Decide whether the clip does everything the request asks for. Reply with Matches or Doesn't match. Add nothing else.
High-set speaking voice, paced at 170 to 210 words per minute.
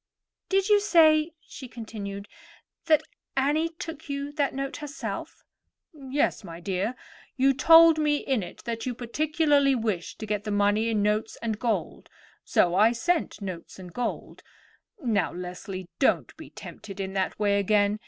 Doesn't match